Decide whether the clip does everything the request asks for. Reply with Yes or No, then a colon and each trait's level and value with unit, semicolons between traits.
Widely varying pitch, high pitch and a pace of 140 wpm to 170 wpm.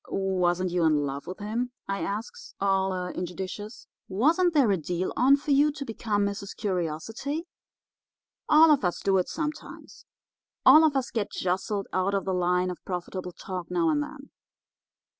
Yes: wide, 7.2 semitones; high, 200 Hz; average, 165 wpm